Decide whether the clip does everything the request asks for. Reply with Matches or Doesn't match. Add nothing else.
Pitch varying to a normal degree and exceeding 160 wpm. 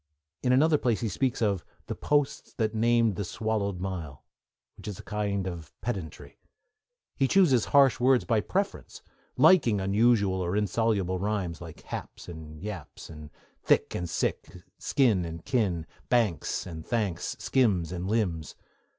Doesn't match